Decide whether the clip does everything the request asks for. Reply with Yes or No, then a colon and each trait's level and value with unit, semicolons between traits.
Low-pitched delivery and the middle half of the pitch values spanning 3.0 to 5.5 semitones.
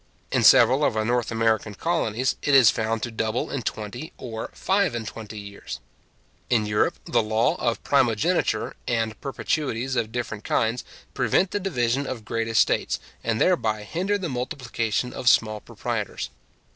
Yes: low, 115 Hz; average, 3.3 semitones